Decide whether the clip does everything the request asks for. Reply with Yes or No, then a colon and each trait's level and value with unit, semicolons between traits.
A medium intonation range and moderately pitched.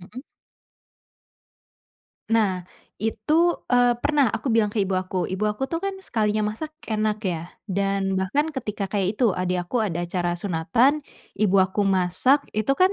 No: average, 4.6 semitones; high, 210 Hz